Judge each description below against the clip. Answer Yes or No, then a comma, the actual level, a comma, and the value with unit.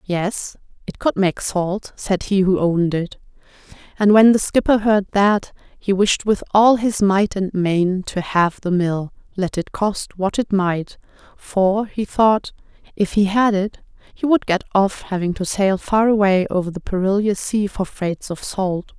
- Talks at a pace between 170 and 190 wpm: Yes, average, 185 wpm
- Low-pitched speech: No, high, 195 Hz